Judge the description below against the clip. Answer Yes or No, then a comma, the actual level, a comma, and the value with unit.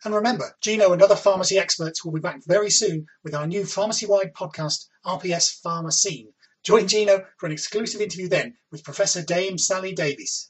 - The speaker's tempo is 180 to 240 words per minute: Yes, average, 185 wpm